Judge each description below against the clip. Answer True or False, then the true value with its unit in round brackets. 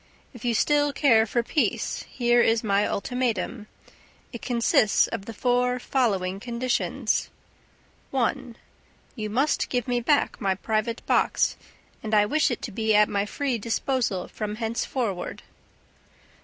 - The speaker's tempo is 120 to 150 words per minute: True (140 wpm)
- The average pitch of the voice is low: False (235 Hz)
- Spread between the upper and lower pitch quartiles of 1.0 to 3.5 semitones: True (2.8 semitones)